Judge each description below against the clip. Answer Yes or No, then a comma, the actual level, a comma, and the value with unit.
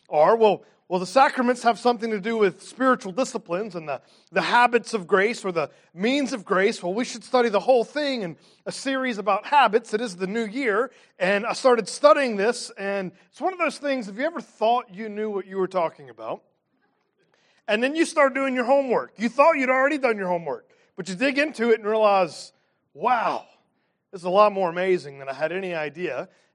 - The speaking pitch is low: No, high, 225 Hz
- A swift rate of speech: Yes, fast, 215 wpm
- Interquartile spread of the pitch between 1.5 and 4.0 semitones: No, average, 5.3 semitones